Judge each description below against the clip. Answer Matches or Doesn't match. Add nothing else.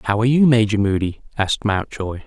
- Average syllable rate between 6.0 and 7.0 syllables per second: Matches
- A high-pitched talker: Doesn't match